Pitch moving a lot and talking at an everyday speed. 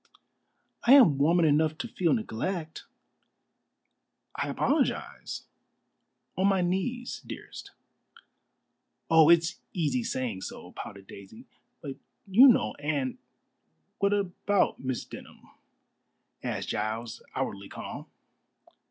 No: wide, 7.1 semitones; slow, 105 wpm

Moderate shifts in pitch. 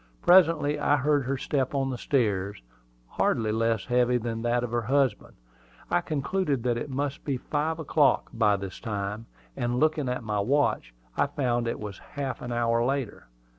Yes: average, 3.9 semitones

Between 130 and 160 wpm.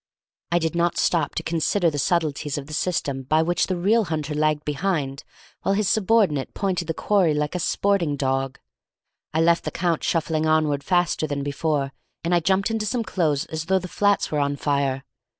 No: average, 195 wpm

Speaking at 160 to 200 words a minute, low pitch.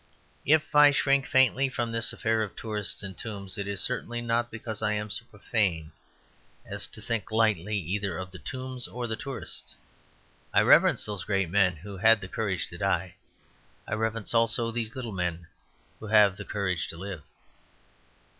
Yes: average, 175 wpm; low, 110 Hz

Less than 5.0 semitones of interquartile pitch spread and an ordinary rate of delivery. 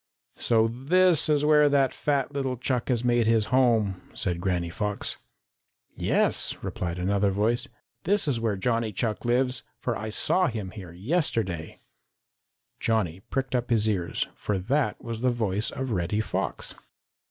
Yes: average, 4.5 semitones; average, 155 wpm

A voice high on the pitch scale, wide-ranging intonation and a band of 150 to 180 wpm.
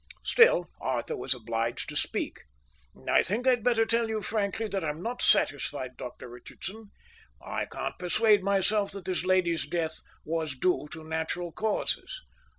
No: medium, 180 Hz; wide, 6.0 semitones; average, 155 wpm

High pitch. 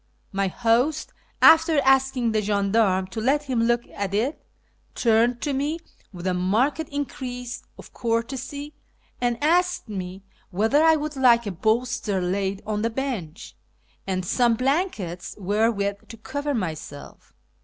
Yes: high, 230 Hz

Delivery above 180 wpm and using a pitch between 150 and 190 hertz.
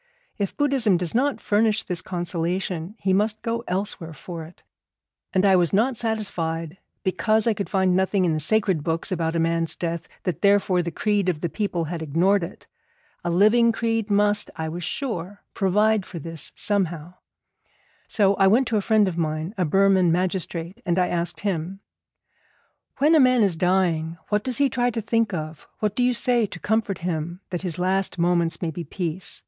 Yes: average, 190 wpm; medium, 185 Hz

